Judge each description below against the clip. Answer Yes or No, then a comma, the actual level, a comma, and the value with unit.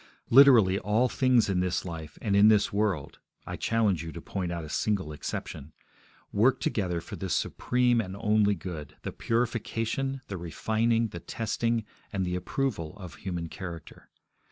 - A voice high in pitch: No, low, 100 Hz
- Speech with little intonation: No, average, 4.7 semitones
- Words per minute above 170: No, average, 160 wpm